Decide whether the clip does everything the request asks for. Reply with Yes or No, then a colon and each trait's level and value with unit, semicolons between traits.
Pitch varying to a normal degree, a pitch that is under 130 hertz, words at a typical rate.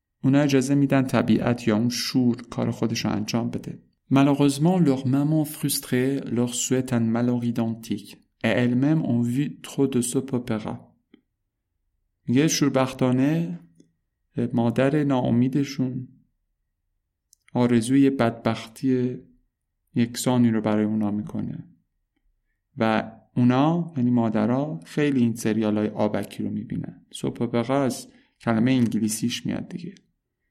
No: average, 3.4 semitones; low, 120 Hz; slow, 100 wpm